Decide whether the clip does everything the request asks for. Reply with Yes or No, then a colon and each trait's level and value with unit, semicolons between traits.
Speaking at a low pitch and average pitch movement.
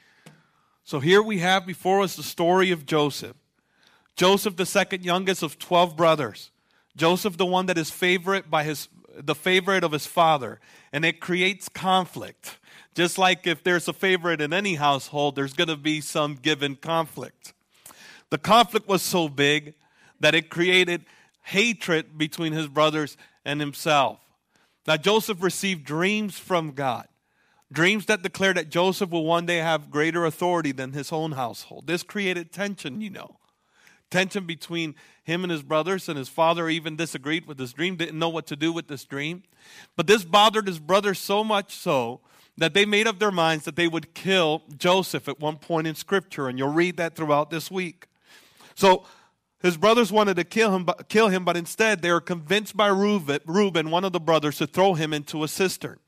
No: medium, 170 Hz; average, 3.4 semitones